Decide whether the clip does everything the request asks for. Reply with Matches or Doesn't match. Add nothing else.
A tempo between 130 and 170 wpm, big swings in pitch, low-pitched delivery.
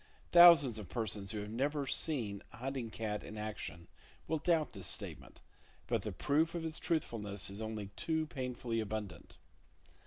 Matches